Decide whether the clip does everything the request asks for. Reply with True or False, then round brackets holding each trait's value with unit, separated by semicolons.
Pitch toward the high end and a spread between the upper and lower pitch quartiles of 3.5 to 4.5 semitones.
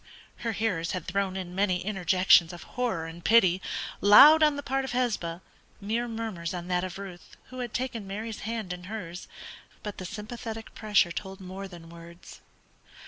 True (195 Hz; 4.1 semitones)